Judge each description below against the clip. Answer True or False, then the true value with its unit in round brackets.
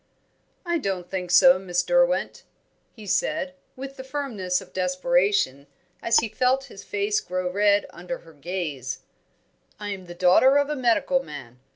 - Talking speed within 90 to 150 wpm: False (160 wpm)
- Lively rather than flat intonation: True (6.5 semitones)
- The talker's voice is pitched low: False (200 Hz)